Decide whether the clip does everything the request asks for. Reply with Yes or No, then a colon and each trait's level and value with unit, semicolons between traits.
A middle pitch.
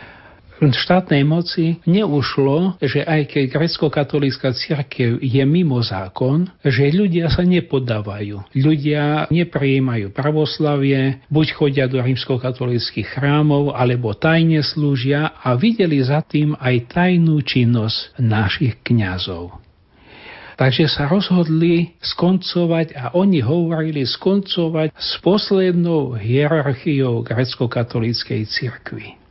Yes: medium, 145 Hz